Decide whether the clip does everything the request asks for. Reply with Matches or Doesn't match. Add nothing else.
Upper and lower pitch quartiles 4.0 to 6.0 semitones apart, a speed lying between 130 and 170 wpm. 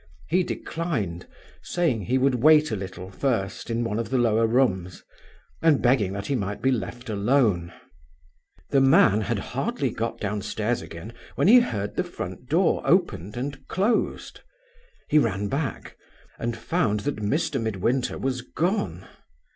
Matches